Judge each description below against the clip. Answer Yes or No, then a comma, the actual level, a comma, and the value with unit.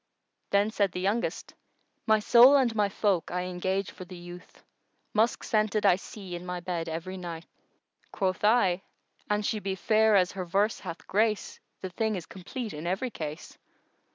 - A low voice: No, high, 195 Hz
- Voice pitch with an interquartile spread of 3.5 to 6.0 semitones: No, average, 3.1 semitones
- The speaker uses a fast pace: No, average, 180 wpm